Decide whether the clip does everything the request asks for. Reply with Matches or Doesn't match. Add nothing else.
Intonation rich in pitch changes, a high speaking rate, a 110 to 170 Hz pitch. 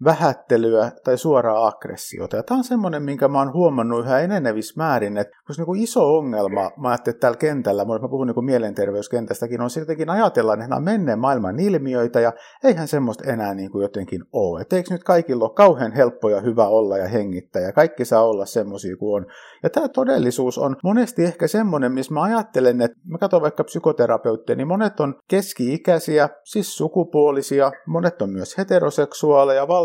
Matches